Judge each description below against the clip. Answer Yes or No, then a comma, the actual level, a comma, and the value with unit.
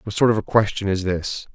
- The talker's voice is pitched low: Yes, low, 100 Hz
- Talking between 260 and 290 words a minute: Yes, fast, 270 wpm